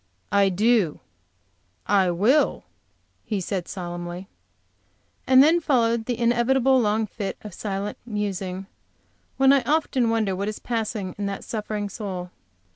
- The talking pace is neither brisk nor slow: No, slow, 130 wpm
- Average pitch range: Yes, average, 3.7 semitones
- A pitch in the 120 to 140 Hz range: No, high, 210 Hz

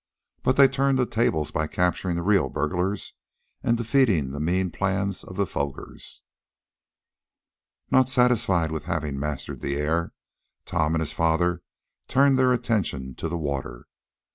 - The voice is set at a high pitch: No, very low, 90 Hz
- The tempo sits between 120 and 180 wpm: Yes, average, 150 wpm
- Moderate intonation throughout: No, wide, 7.2 semitones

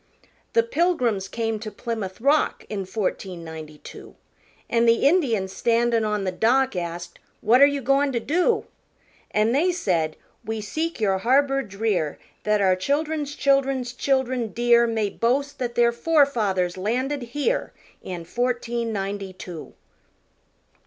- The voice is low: No, high, 235 Hz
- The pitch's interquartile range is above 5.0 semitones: Yes, wide, 5.6 semitones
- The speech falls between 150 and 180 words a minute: No, average, 140 wpm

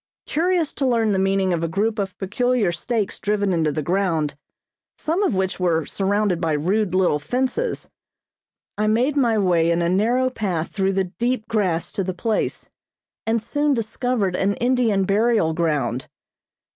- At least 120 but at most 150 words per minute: No, average, 165 wpm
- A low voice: No, high, 200 Hz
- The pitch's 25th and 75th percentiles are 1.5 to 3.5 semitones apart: No, average, 5.0 semitones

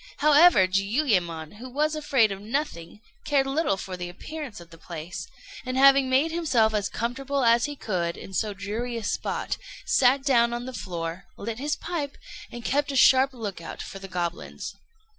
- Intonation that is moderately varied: No, wide, 6.3 semitones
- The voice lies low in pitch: No, high, 235 Hz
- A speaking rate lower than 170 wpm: No, average, 180 wpm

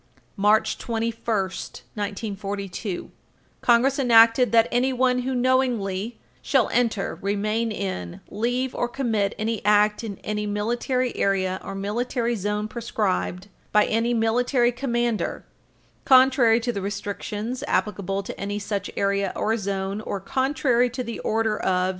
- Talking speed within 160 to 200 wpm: No, slow, 135 wpm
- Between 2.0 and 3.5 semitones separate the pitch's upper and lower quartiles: Yes, average, 3.2 semitones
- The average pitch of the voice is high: Yes, high, 220 Hz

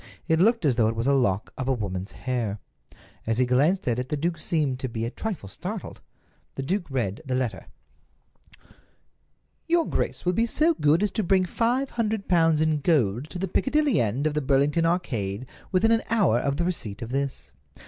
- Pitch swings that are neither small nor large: No, wide, 7.1 semitones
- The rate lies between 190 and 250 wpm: Yes, average, 200 wpm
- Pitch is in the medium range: Yes, medium, 145 Hz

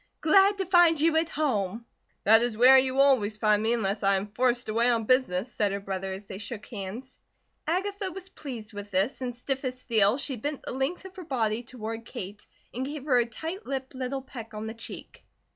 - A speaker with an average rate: No, fast, 220 wpm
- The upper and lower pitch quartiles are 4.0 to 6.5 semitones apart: Yes, average, 4.5 semitones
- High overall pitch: Yes, high, 245 Hz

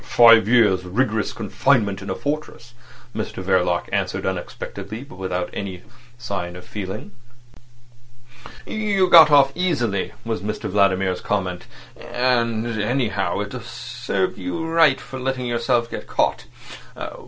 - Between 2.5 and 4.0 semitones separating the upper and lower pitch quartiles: No, average, 5.2 semitones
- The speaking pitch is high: No, low, 115 Hz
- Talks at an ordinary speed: No, slow, 125 wpm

